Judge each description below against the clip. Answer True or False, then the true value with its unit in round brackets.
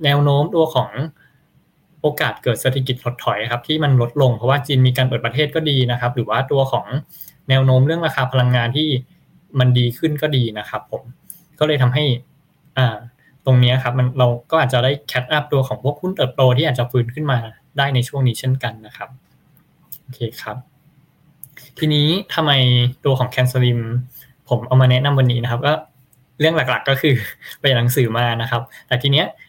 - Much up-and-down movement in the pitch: False (2.9 semitones)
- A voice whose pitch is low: True (130 Hz)